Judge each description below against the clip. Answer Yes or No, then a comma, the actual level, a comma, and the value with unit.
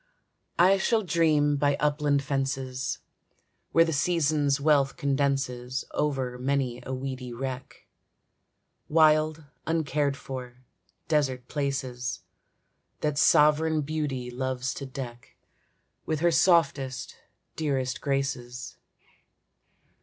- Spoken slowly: Yes, slow, 95 wpm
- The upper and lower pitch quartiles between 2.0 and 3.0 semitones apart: Yes, average, 2.7 semitones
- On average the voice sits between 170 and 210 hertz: No, medium, 140 Hz